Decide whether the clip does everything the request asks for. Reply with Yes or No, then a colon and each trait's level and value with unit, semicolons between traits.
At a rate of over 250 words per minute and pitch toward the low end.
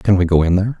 Yes: fast, 375 wpm; very low, 95 Hz